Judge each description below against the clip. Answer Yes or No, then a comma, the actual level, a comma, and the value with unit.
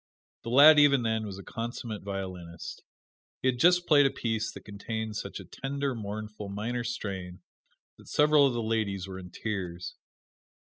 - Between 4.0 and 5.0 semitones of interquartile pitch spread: Yes, average, 4.7 semitones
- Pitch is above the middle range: No, low, 110 Hz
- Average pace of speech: Yes, average, 170 wpm